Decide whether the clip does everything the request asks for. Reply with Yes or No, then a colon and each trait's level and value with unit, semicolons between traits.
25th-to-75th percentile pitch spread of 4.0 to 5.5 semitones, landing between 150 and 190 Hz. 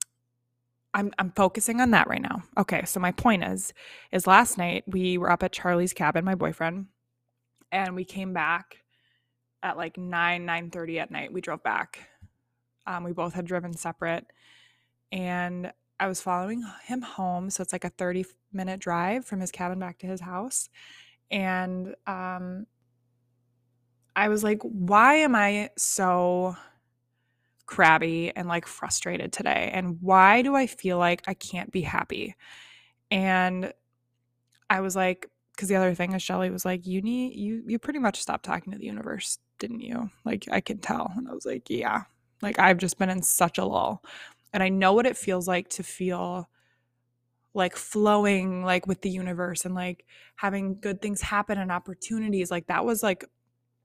No: narrow, 2.5 semitones; medium, 185 Hz